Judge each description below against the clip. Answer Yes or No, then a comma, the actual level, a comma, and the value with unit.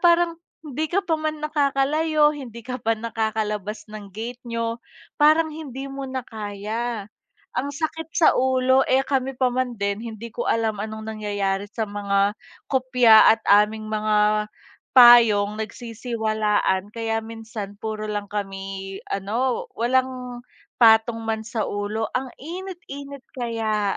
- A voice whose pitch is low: No, high, 230 Hz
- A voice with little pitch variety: No, average, 3.7 semitones